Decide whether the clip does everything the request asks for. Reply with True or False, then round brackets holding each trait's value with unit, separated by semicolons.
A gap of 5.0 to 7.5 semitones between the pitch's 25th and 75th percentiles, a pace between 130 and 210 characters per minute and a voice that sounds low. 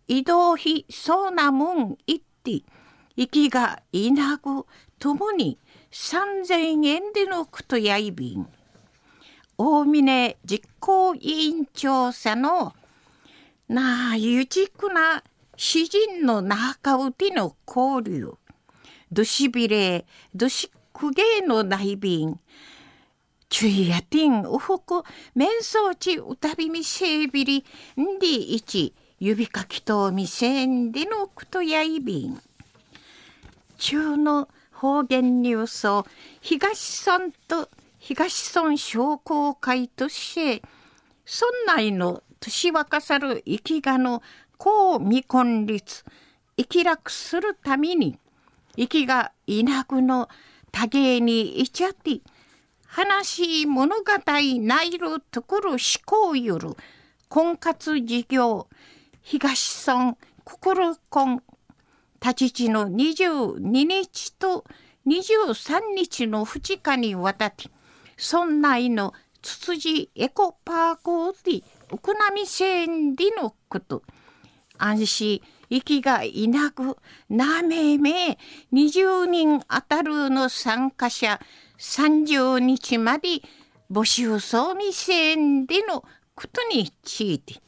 False (5.7 semitones; 170 characters per minute; 290 Hz)